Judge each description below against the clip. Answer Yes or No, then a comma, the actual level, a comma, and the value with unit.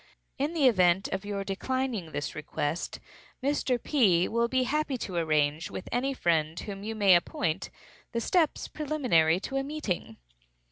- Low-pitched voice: No, high, 205 Hz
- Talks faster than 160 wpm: No, average, 155 wpm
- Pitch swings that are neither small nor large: No, wide, 7.6 semitones